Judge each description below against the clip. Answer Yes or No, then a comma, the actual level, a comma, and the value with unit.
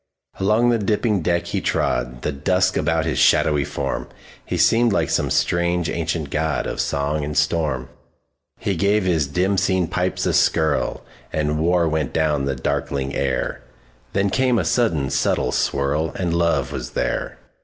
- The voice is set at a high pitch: No, very low, 80 Hz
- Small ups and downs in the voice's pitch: No, average, 4.7 semitones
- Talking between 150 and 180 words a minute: No, average, 140 wpm